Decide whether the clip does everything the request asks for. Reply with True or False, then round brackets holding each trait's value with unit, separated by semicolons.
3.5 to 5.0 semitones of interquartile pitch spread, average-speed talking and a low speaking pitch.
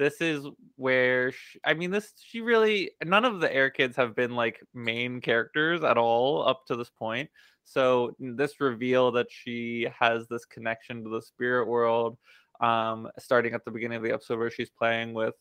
False (2.7 semitones; 190 wpm; 120 Hz)